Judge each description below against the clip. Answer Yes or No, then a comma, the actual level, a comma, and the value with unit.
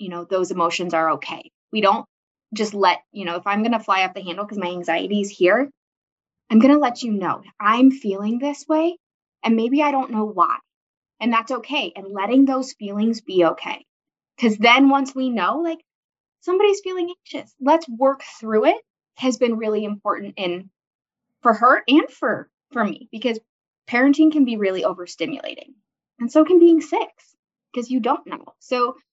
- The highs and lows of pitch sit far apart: Yes, wide, 5.8 semitones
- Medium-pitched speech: No, high, 240 Hz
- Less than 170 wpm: No, average, 185 wpm